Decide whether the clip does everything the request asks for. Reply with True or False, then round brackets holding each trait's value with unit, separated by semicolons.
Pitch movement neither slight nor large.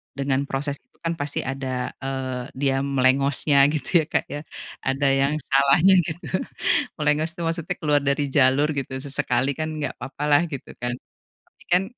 False (2.0 semitones)